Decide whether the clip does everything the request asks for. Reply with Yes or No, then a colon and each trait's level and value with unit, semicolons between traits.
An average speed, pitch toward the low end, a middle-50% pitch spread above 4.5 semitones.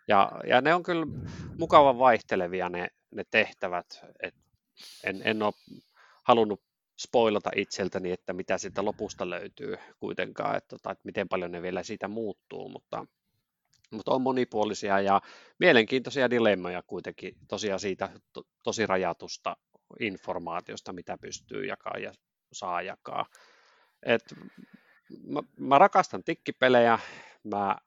Yes: average, 125 wpm; low, 110 Hz; wide, 5.4 semitones